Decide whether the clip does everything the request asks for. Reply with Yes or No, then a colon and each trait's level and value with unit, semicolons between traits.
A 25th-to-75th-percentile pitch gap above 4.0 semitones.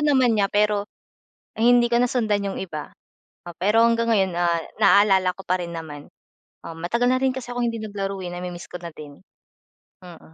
Yes: average, 4.9 semitones